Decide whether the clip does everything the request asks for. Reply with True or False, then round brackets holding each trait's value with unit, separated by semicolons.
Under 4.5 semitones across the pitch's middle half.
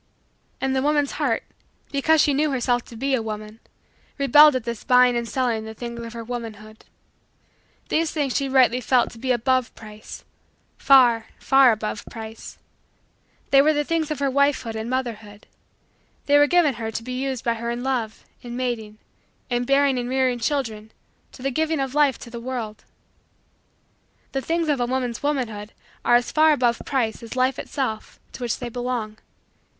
True (3.1 semitones)